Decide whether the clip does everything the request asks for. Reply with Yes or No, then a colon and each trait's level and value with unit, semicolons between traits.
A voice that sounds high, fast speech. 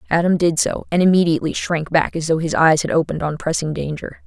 No: medium, 160 Hz; fast, 225 wpm